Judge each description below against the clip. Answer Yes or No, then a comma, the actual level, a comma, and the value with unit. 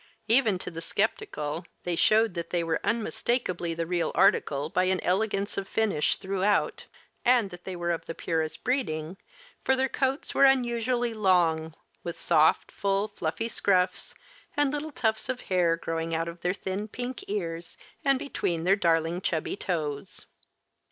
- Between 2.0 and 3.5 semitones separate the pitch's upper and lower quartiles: No, average, 5.2 semitones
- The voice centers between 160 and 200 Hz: Yes, medium, 185 Hz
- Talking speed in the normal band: Yes, average, 160 wpm